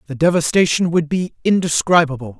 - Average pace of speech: No, slow, 125 wpm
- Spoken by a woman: No, male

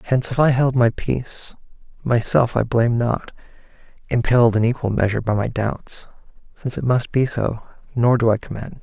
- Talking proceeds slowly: No, average, 175 wpm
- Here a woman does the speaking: No, male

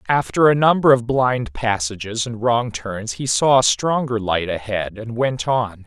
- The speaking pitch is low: Yes, low, 115 Hz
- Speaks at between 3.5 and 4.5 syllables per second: Yes, 4.2 syllables/s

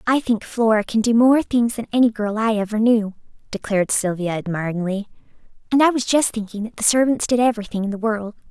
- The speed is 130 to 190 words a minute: No, fast, 205 wpm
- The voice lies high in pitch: Yes, high, 220 Hz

